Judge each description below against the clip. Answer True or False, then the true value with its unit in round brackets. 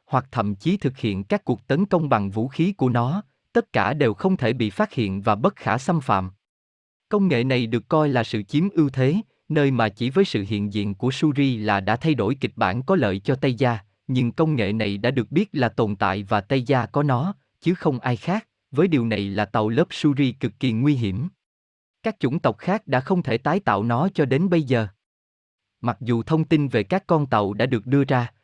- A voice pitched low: True (125 Hz)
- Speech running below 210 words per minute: False (240 wpm)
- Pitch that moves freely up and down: True (6.2 semitones)